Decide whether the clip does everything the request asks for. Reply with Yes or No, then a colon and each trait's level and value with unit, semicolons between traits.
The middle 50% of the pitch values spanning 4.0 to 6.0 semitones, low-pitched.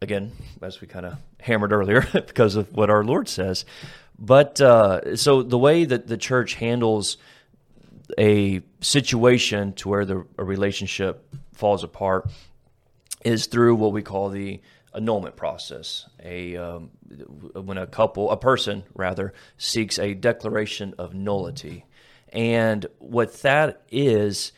No: average, 3.2 semitones; low, 105 Hz